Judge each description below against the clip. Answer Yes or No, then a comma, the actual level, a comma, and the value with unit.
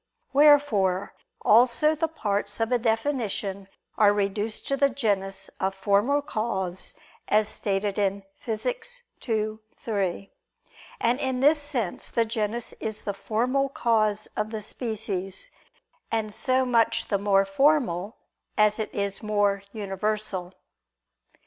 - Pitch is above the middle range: Yes, high, 215 Hz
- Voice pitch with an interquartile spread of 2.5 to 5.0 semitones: Yes, average, 3.2 semitones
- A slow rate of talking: Yes, slow, 130 wpm